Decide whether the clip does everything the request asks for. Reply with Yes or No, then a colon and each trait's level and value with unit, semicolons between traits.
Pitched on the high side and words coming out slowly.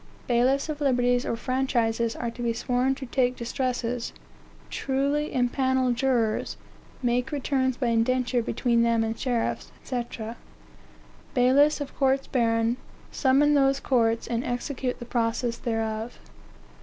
Yes: high, 245 Hz; slow, 130 wpm